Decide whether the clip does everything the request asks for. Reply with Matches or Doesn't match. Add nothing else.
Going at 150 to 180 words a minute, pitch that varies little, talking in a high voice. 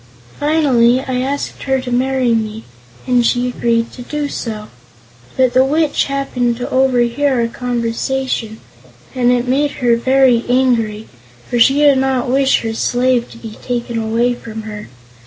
Matches